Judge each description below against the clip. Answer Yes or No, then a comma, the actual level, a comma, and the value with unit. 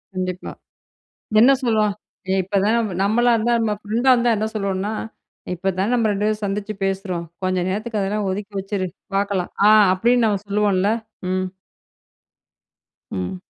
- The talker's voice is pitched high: Yes, high, 205 Hz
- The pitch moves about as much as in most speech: No, narrow, 2.3 semitones